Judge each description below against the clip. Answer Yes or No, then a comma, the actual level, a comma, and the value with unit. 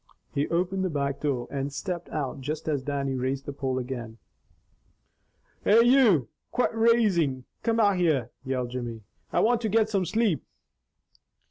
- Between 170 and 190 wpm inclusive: No, average, 155 wpm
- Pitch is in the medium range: Yes, medium, 150 Hz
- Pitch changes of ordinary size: No, wide, 7.5 semitones